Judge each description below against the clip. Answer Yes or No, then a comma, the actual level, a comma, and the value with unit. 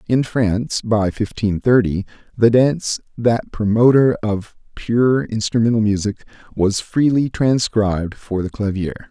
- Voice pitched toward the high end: No, low, 110 Hz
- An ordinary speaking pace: No, slow, 125 wpm